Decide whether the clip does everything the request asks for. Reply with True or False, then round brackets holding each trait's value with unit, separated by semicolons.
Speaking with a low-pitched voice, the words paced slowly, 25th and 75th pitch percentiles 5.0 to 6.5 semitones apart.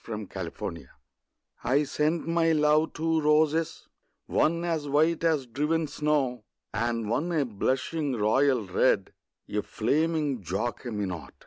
False (145 Hz; 125 wpm; 5.4 semitones)